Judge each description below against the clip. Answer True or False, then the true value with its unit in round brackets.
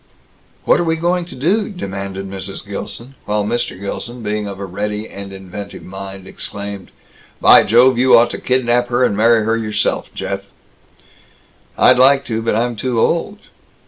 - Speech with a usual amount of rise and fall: True (4.1 semitones)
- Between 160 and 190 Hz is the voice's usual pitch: False (110 Hz)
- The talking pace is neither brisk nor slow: True (170 wpm)